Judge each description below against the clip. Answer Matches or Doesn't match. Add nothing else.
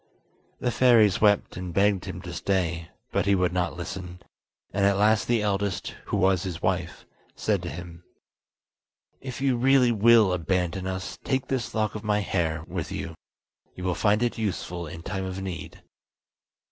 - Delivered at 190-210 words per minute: Doesn't match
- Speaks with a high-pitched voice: Doesn't match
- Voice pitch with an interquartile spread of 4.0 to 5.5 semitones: Doesn't match